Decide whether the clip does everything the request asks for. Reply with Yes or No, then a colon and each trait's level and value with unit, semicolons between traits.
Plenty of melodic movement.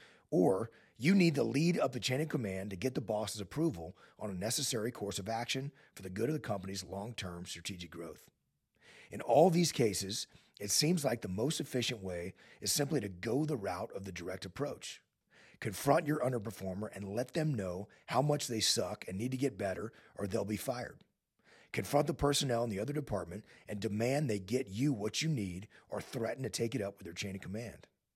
Yes: wide, 6.5 semitones